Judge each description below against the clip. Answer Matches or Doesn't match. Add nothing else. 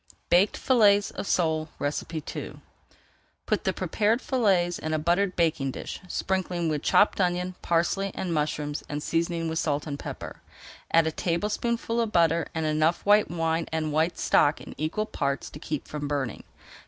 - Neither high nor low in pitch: Matches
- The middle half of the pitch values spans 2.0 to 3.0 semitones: Doesn't match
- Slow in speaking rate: Doesn't match